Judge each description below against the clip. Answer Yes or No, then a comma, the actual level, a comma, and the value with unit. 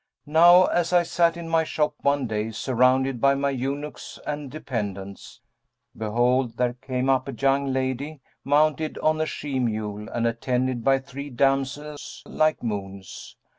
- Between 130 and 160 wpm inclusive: Yes, average, 150 wpm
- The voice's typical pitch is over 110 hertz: Yes, low, 135 Hz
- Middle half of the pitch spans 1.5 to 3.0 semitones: No, average, 3.5 semitones